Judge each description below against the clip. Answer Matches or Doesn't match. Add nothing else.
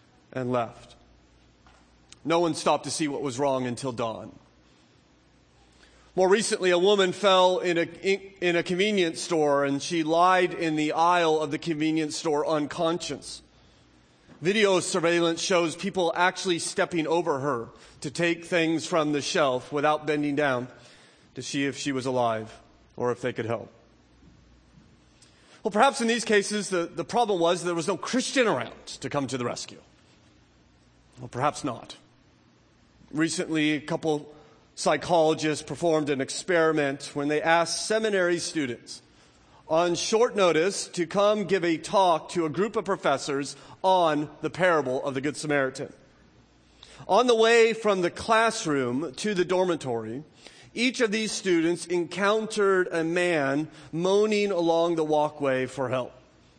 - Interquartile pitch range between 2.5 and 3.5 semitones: Doesn't match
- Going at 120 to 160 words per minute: Matches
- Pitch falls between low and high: Matches